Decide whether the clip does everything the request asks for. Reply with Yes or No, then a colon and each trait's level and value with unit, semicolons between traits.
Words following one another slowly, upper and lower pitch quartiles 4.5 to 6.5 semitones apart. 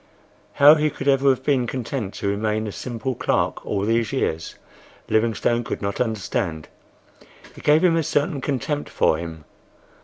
No: average, 160 wpm; average, 5.2 semitones